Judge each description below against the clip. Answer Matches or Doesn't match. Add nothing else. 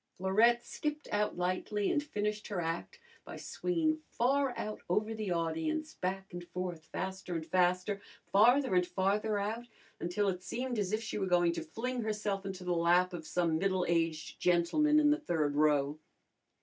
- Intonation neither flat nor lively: Matches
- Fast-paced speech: Doesn't match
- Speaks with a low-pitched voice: Doesn't match